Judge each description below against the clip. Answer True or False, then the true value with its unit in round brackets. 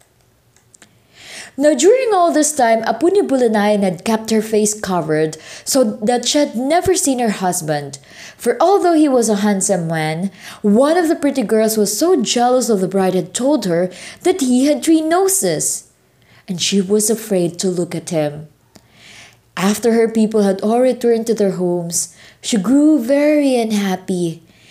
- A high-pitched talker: True (220 Hz)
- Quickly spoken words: False (165 wpm)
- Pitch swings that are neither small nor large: False (6.8 semitones)